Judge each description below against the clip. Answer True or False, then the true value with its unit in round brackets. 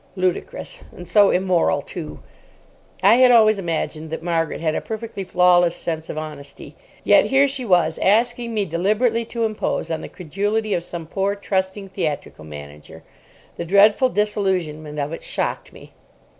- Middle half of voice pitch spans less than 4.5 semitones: False (4.8 semitones)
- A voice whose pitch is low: False (185 Hz)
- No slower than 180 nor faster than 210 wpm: False (155 wpm)